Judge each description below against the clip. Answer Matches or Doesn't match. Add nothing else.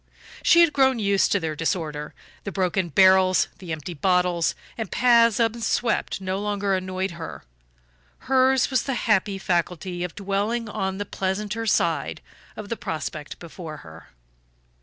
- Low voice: Doesn't match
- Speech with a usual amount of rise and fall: Matches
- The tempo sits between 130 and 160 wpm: Matches